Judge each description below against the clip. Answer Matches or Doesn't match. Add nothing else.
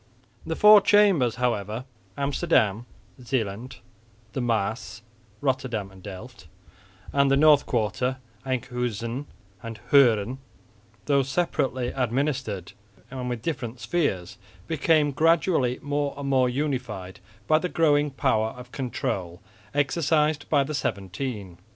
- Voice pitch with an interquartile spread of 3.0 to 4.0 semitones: Doesn't match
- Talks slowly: Matches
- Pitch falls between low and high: Doesn't match